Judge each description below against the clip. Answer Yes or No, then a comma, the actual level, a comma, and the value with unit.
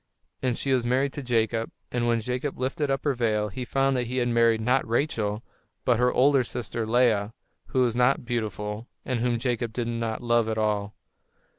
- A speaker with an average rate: Yes, average, 195 wpm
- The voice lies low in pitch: Yes, low, 120 Hz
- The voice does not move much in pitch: Yes, narrow, 2.1 semitones